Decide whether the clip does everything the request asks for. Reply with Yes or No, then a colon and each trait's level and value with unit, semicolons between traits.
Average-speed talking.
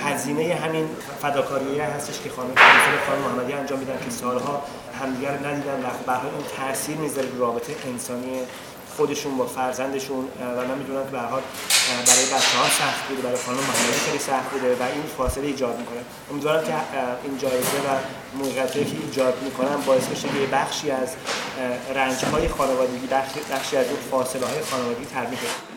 Yes: average, 160 wpm